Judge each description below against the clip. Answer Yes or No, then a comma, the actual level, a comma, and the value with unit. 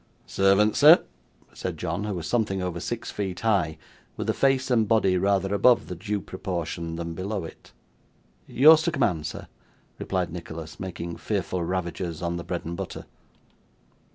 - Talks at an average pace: Yes, average, 160 wpm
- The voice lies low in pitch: Yes, very low, 95 Hz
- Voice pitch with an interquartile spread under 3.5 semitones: No, average, 3.9 semitones